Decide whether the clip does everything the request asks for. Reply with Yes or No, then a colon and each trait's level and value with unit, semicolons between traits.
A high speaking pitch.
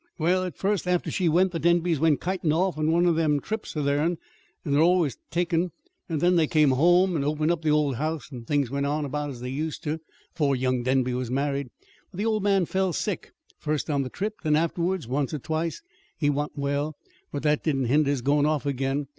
No: medium, 155 Hz